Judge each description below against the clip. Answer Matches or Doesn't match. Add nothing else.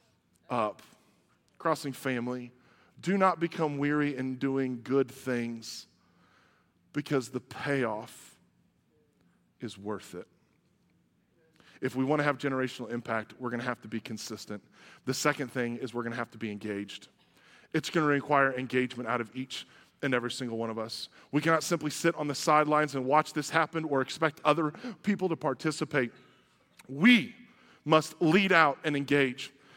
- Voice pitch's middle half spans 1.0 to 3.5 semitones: Doesn't match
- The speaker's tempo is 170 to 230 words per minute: Doesn't match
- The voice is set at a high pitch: Doesn't match